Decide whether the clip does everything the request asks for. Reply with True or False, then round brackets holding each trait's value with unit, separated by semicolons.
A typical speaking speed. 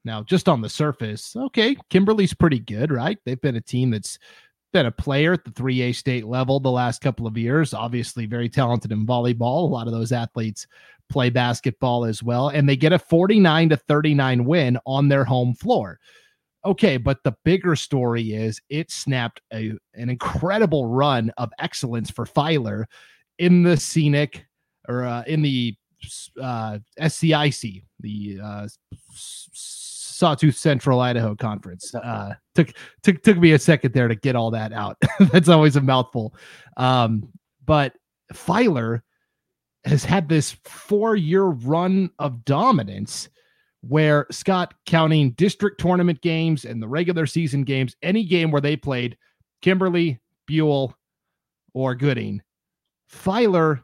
True (150 wpm)